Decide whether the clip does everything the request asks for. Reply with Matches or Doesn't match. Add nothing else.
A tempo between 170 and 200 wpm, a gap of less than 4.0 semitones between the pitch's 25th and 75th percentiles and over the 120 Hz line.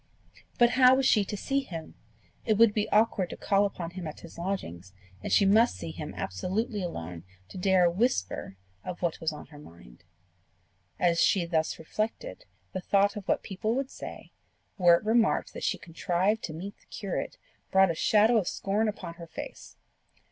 Doesn't match